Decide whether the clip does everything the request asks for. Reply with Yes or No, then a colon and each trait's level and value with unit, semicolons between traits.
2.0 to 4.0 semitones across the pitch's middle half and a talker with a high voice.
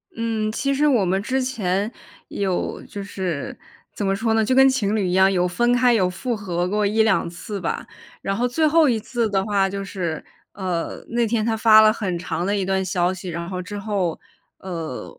Yes: average, 3.6 semitones; high, 200 Hz